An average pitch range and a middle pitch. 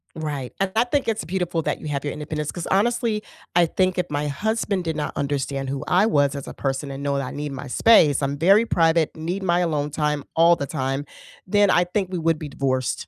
Yes: average, 4.6 semitones; medium, 160 Hz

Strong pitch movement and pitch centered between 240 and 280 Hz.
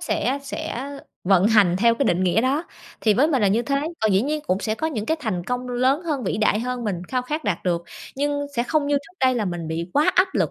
Yes: wide, 6.0 semitones; high, 245 Hz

